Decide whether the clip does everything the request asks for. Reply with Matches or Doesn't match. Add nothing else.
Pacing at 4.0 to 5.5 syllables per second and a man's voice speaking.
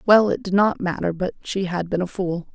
Doesn't match